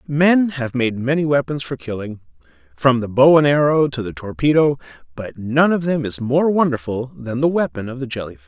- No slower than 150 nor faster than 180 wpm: No, fast, 205 wpm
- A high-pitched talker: No, low, 130 Hz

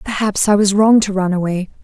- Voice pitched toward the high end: Yes, high, 200 Hz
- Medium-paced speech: No, fast, 230 wpm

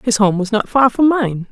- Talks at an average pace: No, fast, 275 wpm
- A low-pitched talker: No, high, 225 Hz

